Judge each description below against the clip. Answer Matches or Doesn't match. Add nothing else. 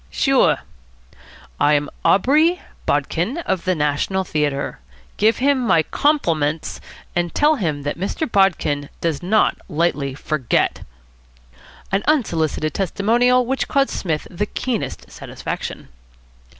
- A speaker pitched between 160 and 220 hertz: Matches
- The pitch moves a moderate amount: Doesn't match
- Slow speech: Matches